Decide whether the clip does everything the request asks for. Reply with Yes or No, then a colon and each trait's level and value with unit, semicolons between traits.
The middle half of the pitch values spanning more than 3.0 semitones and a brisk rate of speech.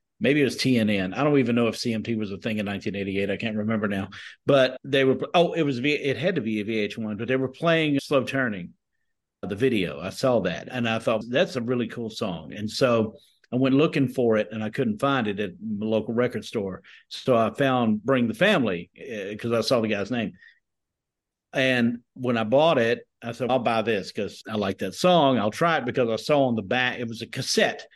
Yes: average, 3.5 semitones; fast, 230 wpm